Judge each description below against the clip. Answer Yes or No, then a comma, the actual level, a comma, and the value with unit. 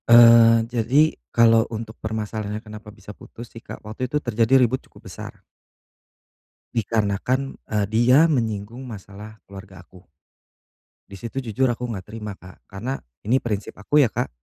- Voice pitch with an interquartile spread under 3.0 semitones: Yes, narrow, 2.4 semitones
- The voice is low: Yes, low, 110 Hz